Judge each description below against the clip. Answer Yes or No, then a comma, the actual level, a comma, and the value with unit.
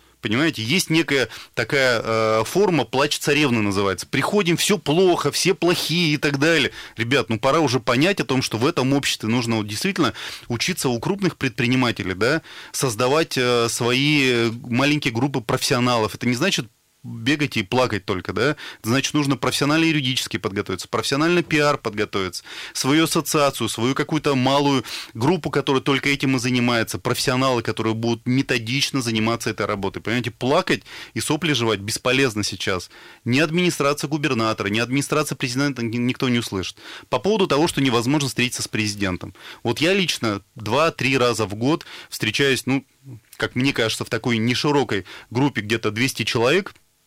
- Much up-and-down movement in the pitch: No, average, 4.2 semitones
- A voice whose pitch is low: Yes, low, 130 Hz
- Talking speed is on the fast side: No, average, 150 wpm